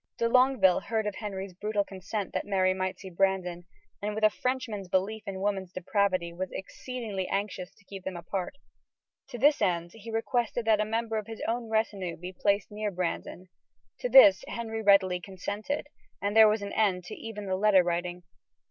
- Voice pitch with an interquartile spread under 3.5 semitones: Yes, average, 2.9 semitones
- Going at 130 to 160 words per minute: No, average, 185 wpm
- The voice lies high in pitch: Yes, high, 200 Hz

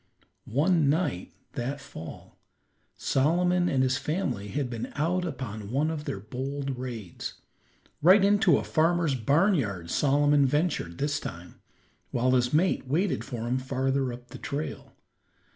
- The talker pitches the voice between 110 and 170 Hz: Yes, medium, 140 Hz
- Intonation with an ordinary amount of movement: Yes, average, 4.5 semitones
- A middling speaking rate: Yes, average, 145 wpm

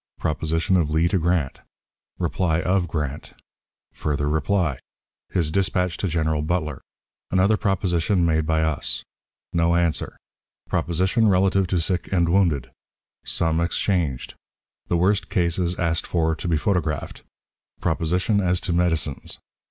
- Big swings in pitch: No, average, 2.7 semitones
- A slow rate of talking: Yes, slow, 130 wpm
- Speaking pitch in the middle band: No, very low, 85 Hz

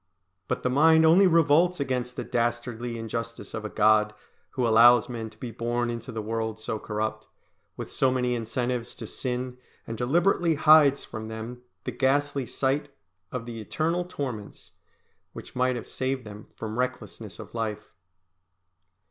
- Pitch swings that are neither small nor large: Yes, average, 3.4 semitones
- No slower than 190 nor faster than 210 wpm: No, average, 155 wpm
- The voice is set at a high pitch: No, low, 120 Hz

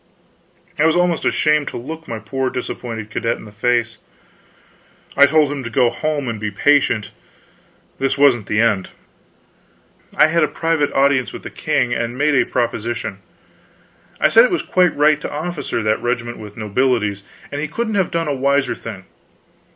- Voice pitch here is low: Yes, low, 130 Hz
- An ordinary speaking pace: Yes, average, 175 wpm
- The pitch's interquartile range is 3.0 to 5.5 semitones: Yes, average, 4.7 semitones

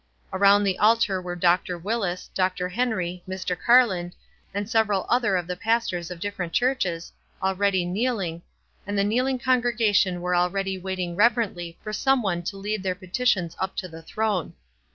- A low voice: No, high, 190 Hz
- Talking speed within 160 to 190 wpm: Yes, average, 165 wpm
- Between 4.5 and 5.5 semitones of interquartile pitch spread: No, average, 3.7 semitones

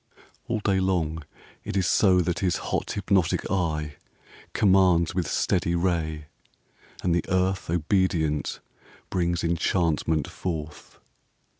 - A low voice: Yes, very low, 85 Hz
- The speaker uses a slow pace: Yes, slow, 120 wpm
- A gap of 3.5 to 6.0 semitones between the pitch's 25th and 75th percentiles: No, narrow, 2.6 semitones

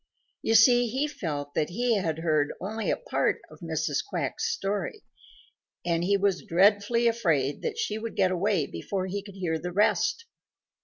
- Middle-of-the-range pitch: No, high, 195 Hz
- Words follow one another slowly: No, average, 170 wpm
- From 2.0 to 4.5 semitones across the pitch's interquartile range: No, average, 4.9 semitones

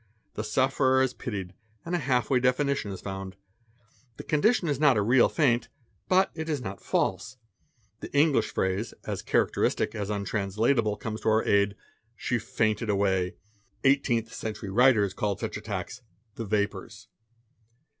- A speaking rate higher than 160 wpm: No, average, 155 wpm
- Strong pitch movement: No, average, 4.6 semitones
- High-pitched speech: No, low, 110 Hz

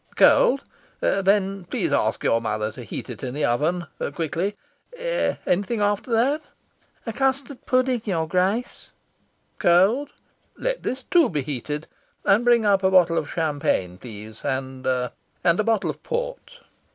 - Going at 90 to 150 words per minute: Yes, average, 145 wpm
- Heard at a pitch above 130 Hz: Yes, high, 190 Hz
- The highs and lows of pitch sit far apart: Yes, wide, 8.6 semitones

